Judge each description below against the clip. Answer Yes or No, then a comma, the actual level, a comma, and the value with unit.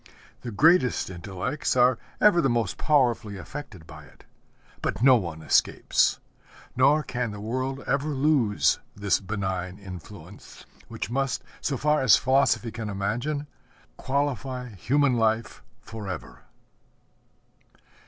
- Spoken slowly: Yes, slow, 120 wpm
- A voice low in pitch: Yes, low, 120 Hz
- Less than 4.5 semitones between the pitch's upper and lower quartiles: No, average, 5.2 semitones